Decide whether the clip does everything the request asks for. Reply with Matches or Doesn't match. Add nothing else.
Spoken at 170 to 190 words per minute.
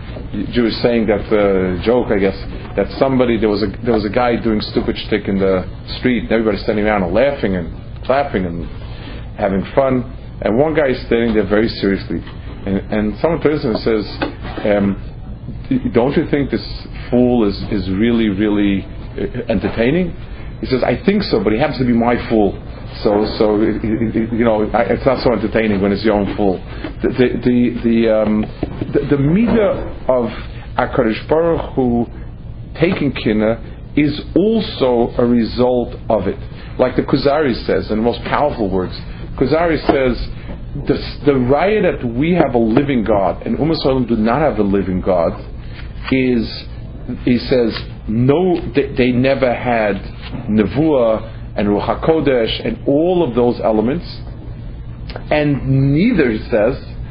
Doesn't match